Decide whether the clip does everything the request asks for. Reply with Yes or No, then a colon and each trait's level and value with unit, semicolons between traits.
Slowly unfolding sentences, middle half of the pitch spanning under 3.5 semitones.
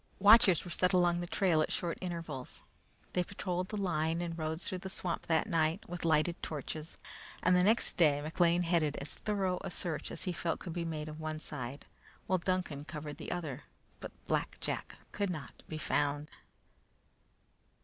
No: average, 180 wpm; average, 2.7 semitones